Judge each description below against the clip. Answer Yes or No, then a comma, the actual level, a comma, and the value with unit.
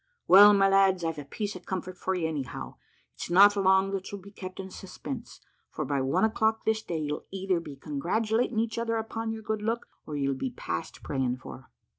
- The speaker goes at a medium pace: No, fast, 210 wpm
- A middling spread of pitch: No, wide, 6.3 semitones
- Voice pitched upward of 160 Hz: Yes, high, 190 Hz